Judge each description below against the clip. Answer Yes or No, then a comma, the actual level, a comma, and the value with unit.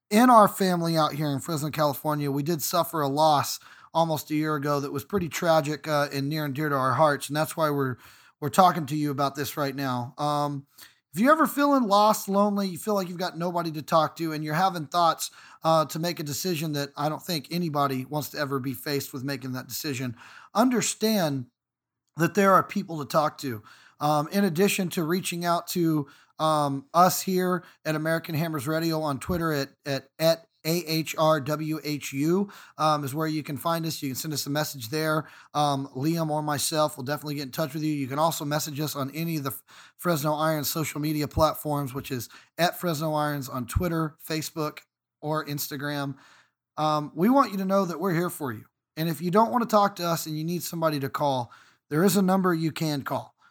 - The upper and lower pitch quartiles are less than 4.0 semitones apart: Yes, average, 2.9 semitones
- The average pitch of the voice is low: No, medium, 155 Hz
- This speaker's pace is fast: Yes, fast, 215 wpm